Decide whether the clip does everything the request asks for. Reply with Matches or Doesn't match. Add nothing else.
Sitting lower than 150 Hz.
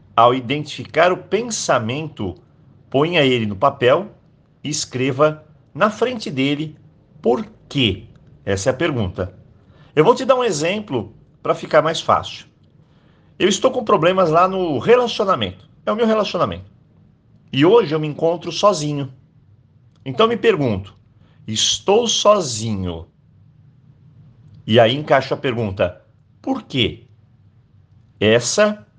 Matches